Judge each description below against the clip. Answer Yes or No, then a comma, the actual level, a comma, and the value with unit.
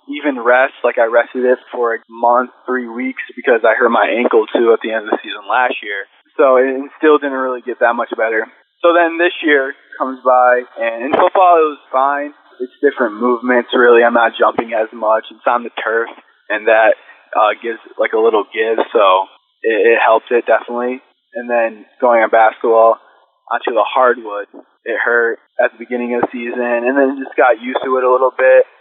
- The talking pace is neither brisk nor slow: No, fast, 210 wpm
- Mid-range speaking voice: No, low, 130 Hz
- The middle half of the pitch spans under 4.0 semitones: No, average, 4.3 semitones